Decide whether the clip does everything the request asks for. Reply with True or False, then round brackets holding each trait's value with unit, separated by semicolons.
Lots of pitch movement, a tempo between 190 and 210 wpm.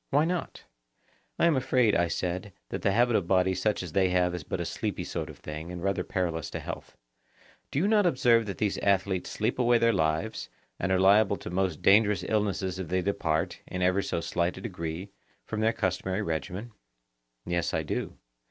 False (3.6 semitones; 200 wpm)